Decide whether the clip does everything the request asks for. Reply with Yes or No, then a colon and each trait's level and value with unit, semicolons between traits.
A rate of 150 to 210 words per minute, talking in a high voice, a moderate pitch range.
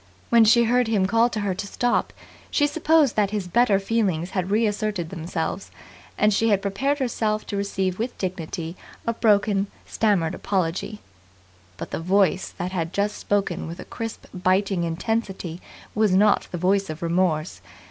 Yes: average, 165 wpm; high, 200 Hz; average, 3.3 semitones